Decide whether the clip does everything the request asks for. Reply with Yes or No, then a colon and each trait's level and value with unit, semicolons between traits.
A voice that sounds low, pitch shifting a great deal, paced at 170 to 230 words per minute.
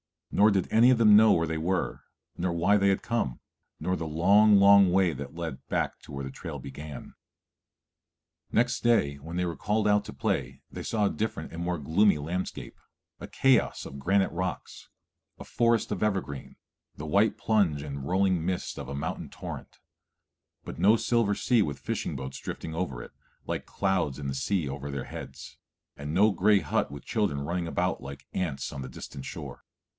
Yes: very low, 90 Hz; wide, 6.1 semitones; average, 190 wpm